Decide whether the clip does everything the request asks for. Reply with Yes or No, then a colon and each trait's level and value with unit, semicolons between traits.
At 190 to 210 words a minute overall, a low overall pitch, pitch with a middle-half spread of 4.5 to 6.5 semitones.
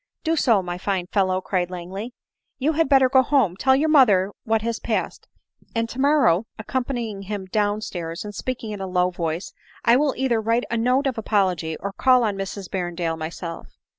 No: average, 200 wpm; high, 210 Hz; wide, 5.5 semitones